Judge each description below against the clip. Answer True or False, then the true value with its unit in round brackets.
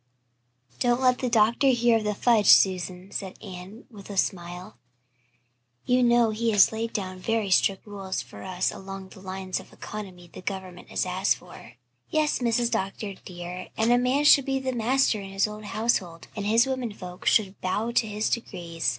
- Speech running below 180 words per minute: False (185 wpm)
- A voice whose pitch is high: True (205 Hz)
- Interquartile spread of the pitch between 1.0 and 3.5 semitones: False (3.9 semitones)